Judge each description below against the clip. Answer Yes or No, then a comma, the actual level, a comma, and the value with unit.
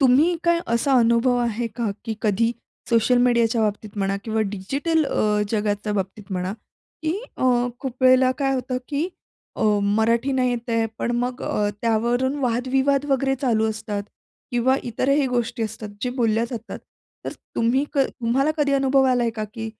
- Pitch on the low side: No, high, 240 Hz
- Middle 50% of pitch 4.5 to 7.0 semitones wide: No, average, 3.1 semitones